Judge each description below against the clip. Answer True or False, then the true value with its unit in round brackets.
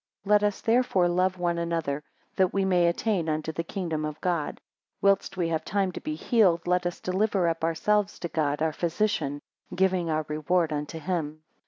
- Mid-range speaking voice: True (175 Hz)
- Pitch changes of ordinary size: True (3.2 semitones)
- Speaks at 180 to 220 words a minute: True (190 wpm)